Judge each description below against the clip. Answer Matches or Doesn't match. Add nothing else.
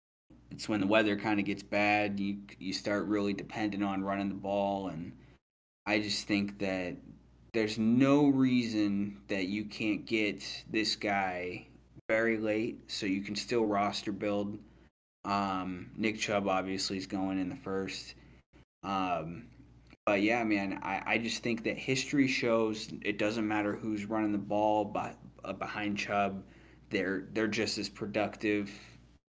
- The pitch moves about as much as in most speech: Doesn't match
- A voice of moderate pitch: Doesn't match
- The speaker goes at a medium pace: Matches